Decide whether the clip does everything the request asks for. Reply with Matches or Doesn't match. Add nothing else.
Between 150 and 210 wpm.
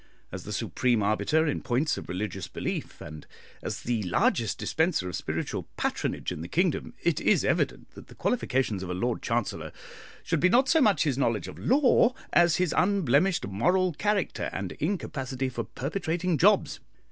Matches